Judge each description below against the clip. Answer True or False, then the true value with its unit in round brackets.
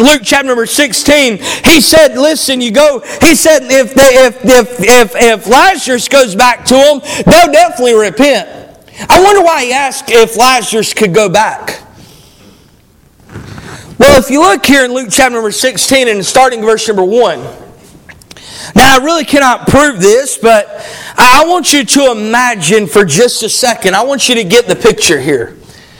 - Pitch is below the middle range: False (260 Hz)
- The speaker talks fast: False (170 wpm)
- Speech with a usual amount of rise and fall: True (4.3 semitones)